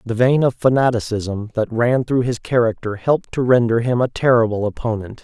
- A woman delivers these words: No, male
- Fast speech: No, average, 185 wpm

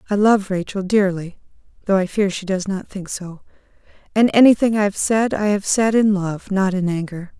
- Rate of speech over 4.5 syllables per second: Yes, 5.0 syllables/s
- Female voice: Yes, female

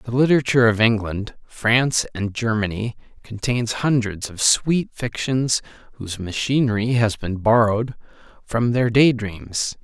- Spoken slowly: Yes, slow, 130 wpm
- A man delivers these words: Yes, male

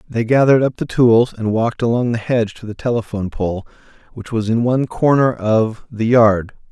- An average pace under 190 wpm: No, average, 195 wpm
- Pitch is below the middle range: Yes, low, 115 Hz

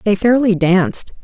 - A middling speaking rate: Yes, average, 145 wpm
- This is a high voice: Yes, high, 200 Hz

